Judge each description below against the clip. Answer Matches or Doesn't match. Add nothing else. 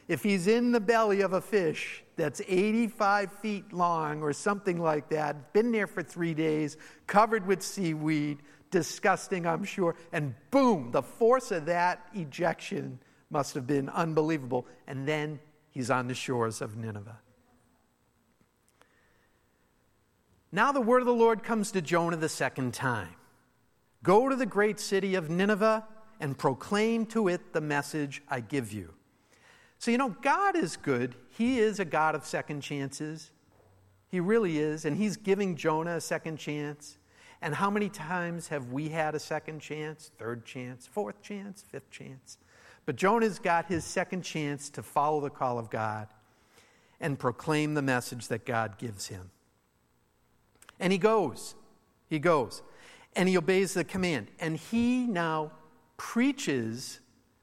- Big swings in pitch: Matches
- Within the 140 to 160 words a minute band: Matches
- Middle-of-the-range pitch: Matches